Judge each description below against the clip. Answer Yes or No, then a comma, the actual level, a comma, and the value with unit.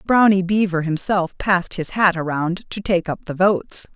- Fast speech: No, average, 180 wpm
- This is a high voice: No, medium, 180 Hz